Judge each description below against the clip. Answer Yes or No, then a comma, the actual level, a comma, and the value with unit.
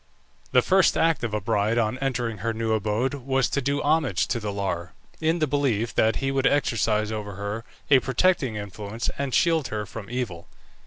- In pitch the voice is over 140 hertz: No, low, 115 Hz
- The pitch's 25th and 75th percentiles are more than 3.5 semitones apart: Yes, average, 4.4 semitones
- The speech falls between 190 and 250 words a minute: Yes, average, 195 wpm